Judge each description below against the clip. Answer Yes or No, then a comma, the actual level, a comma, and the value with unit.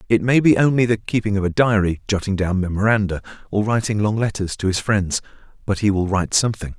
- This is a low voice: Yes, low, 105 Hz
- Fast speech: Yes, fast, 210 wpm